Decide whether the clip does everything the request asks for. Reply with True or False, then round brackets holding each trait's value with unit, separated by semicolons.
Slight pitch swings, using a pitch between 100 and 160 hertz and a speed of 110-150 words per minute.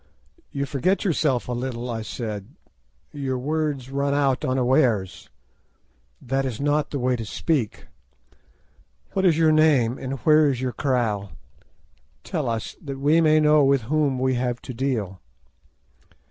False (3.4 semitones; 135 Hz; 145 wpm)